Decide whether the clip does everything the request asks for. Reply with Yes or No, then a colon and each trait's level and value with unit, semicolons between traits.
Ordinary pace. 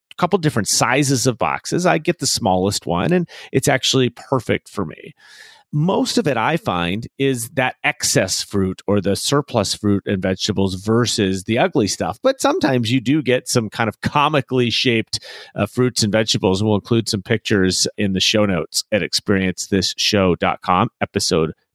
Yes: average, 165 wpm